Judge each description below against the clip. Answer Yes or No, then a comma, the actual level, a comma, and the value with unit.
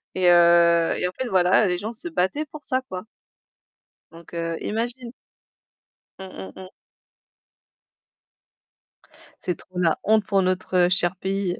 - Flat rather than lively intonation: No, average, 3.7 semitones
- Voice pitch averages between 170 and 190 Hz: Yes, medium, 185 Hz